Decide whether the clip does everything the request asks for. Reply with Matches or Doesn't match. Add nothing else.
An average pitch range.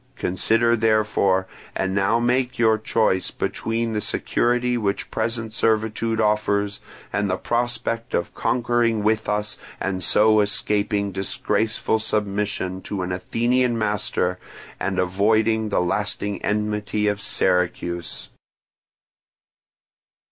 Doesn't match